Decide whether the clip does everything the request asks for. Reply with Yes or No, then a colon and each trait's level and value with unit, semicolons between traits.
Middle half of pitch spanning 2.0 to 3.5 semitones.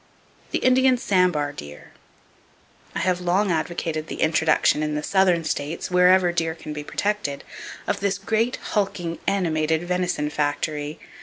No: average, 3.9 semitones